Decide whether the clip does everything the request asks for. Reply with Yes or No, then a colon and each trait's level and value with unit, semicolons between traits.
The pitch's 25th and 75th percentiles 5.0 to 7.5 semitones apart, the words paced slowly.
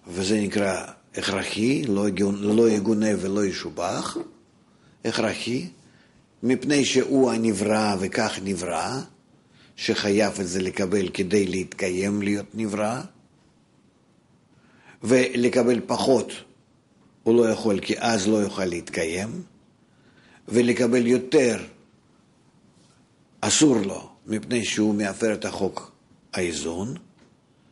No: average, 2.8 semitones; slow, 90 wpm